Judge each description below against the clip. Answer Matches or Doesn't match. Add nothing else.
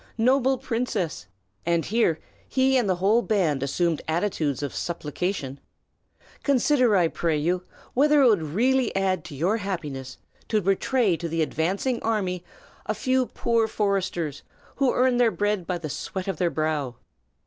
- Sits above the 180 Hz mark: Matches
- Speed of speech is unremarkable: Matches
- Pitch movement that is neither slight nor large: Doesn't match